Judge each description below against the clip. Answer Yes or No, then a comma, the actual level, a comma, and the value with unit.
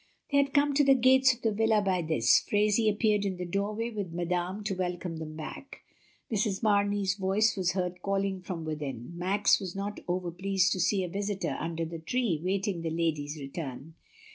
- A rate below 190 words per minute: No, average, 195 wpm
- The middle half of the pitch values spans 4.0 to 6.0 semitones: No, average, 3.5 semitones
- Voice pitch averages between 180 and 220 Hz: Yes, high, 190 Hz